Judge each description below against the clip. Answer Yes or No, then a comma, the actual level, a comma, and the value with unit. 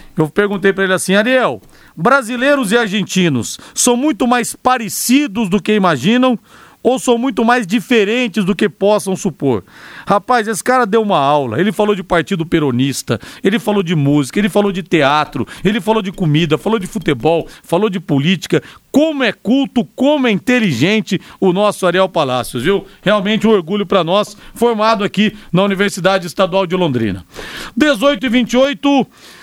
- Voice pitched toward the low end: No, high, 205 Hz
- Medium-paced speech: Yes, average, 165 wpm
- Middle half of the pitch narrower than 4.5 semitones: No, average, 5.0 semitones